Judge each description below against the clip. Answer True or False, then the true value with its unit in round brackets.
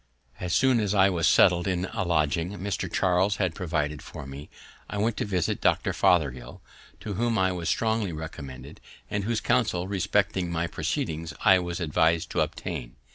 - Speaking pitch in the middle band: False (90 Hz)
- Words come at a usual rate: True (175 wpm)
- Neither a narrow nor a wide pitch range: True (3.9 semitones)